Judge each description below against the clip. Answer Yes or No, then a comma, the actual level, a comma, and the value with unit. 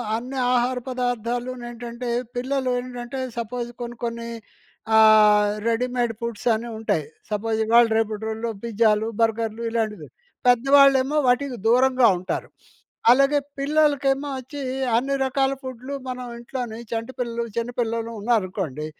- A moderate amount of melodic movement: No, narrow, 2.3 semitones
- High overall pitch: Yes, high, 240 Hz